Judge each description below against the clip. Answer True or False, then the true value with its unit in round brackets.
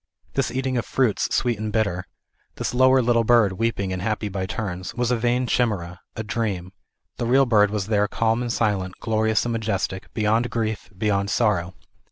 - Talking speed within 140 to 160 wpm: False (190 wpm)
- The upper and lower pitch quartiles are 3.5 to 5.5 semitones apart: False (3.1 semitones)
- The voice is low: True (110 Hz)